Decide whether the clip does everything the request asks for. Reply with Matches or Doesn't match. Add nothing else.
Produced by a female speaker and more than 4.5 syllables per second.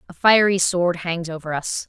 Matches